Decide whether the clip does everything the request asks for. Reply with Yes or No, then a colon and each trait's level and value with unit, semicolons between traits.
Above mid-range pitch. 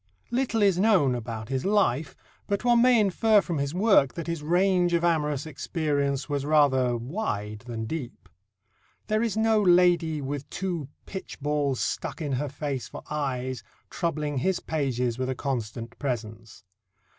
No: medium, 150 Hz